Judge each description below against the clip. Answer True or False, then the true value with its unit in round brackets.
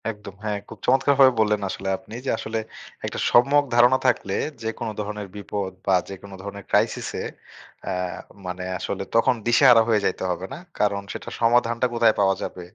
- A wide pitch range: False (3.2 semitones)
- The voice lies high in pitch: False (105 Hz)